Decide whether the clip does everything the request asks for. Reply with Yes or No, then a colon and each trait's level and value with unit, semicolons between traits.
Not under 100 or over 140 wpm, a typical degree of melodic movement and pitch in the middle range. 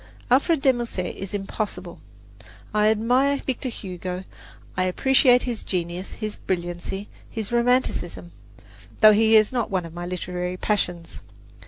No: slow, 135 wpm; average, 4.9 semitones; high, 205 Hz